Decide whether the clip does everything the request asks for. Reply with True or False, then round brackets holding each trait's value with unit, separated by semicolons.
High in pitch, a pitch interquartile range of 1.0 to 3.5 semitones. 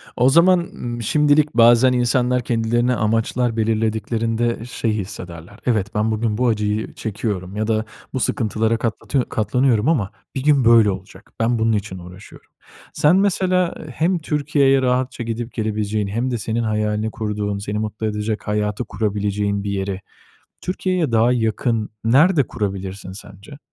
False (115 Hz; 3.1 semitones)